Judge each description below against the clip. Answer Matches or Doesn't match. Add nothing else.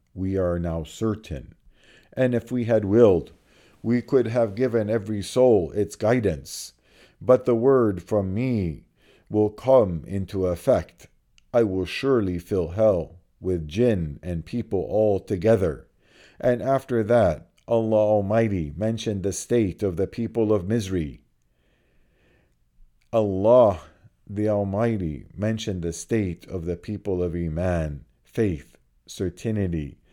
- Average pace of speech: Doesn't match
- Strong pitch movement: Doesn't match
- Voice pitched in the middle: Doesn't match